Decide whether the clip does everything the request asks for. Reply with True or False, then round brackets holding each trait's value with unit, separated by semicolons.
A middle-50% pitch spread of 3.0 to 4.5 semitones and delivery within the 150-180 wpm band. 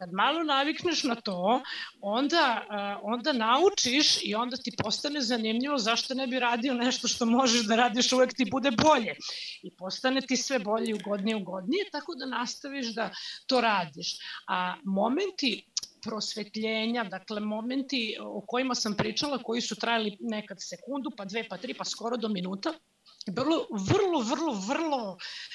True (4.2 semitones; 155 wpm)